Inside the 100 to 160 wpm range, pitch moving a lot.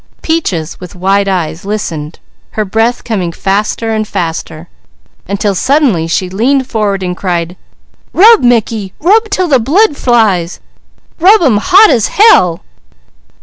Yes: slow, 135 wpm; wide, 7.1 semitones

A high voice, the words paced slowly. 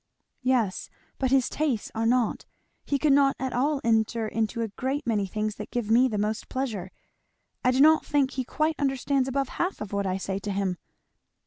No: high, 245 Hz; average, 200 wpm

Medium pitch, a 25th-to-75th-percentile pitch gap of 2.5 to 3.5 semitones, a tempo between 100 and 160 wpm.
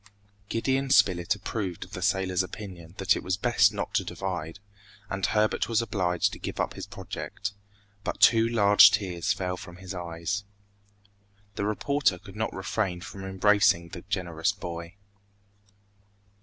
No: very low, 95 Hz; average, 2.8 semitones; average, 150 wpm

